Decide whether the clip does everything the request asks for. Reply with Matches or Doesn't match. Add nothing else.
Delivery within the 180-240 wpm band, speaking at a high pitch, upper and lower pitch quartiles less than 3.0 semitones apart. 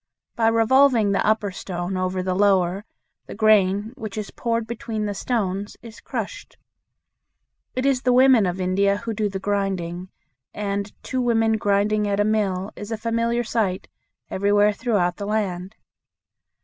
Doesn't match